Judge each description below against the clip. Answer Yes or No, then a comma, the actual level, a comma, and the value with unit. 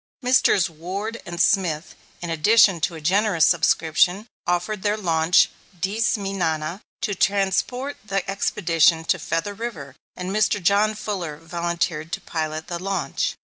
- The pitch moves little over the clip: No, average, 3.8 semitones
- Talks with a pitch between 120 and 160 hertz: No, medium, 180 Hz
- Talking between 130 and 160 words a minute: Yes, average, 140 wpm